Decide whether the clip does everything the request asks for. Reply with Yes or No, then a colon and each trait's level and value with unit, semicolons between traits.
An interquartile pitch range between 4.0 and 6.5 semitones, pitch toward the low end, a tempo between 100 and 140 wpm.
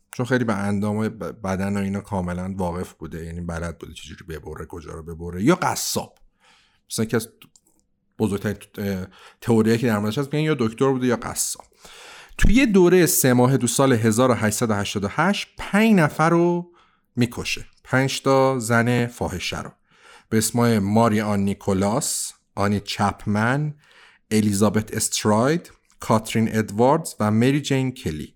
Yes: average, 4.5 semitones; low, 110 Hz; average, 135 wpm